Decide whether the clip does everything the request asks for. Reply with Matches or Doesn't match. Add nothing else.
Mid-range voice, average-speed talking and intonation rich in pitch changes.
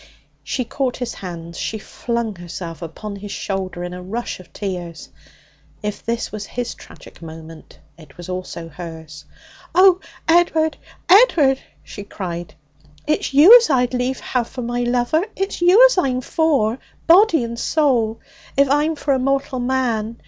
Doesn't match